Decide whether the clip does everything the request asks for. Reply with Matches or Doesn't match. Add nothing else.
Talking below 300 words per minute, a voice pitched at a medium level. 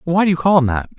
Doesn't match